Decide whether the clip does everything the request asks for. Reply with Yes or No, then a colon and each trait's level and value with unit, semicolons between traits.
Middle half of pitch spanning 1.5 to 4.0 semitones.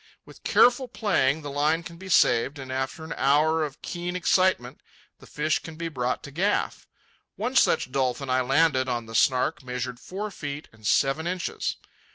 No: average, 4.5 semitones